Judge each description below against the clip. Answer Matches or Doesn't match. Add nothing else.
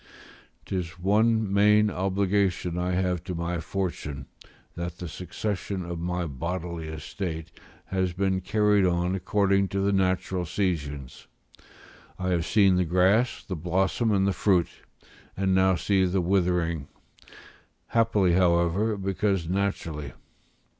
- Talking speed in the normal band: Doesn't match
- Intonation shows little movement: Matches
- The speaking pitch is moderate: Doesn't match